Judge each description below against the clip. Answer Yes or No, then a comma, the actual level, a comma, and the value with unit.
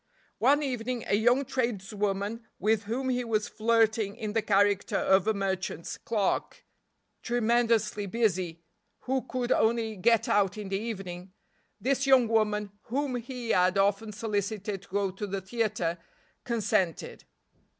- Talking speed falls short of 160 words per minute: Yes, average, 140 wpm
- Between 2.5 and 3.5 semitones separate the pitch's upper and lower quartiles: Yes, average, 3.0 semitones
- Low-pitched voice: No, high, 215 Hz